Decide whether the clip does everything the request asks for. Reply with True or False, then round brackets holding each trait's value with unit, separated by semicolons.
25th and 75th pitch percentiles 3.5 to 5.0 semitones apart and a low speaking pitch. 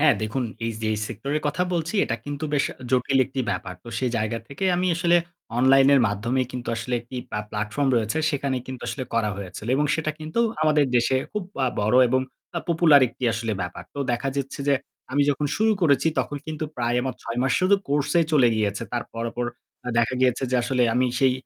True (3.8 semitones; 130 Hz)